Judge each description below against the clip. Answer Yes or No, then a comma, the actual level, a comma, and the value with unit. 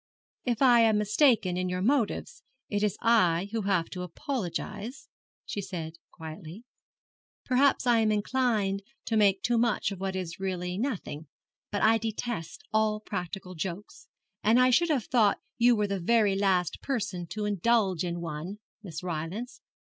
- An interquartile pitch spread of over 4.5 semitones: No, average, 4.2 semitones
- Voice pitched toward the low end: No, high, 205 Hz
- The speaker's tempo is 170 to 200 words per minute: No, average, 160 wpm